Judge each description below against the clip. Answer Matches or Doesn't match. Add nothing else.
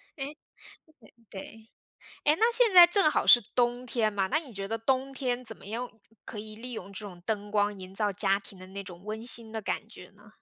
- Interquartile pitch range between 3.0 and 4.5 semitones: Matches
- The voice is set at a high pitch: Matches